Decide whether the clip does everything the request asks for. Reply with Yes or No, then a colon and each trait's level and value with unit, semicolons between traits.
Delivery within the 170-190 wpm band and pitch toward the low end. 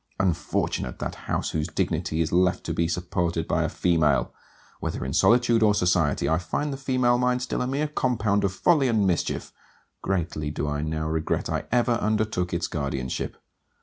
Yes: average, 180 wpm; very low, 90 Hz